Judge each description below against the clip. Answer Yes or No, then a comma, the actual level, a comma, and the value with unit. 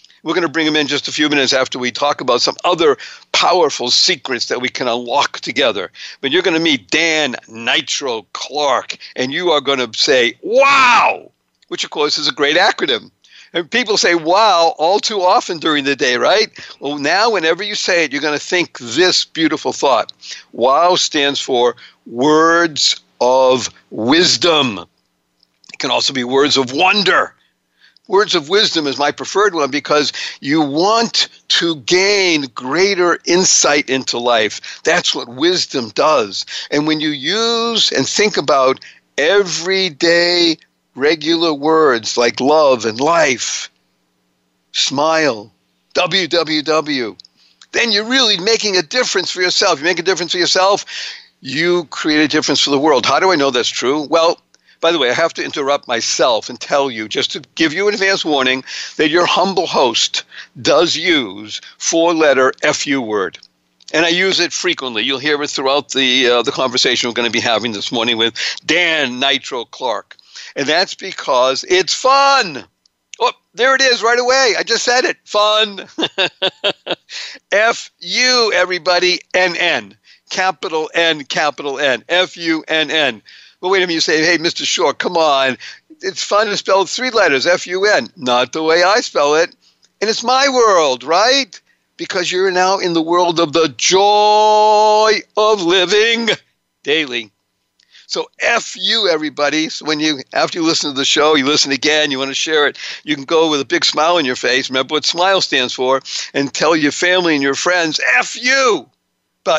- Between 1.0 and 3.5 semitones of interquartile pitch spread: No, wide, 5.5 semitones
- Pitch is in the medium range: Yes, medium, 165 Hz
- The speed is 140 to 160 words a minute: No, average, 175 wpm